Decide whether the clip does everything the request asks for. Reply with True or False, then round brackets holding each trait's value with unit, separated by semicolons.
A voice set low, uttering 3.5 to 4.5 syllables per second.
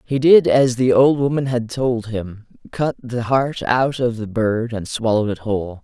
True (120 Hz; 4.4 syllables/s)